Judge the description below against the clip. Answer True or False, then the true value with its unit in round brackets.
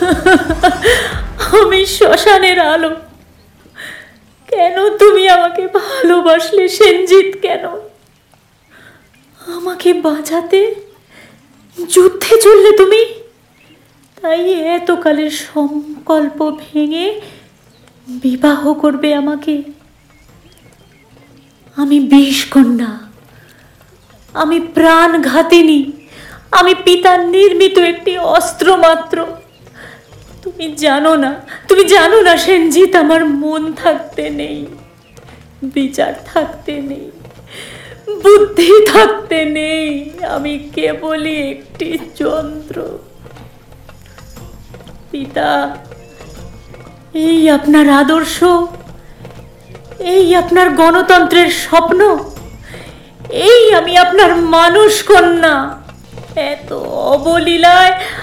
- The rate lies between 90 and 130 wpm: False (70 wpm)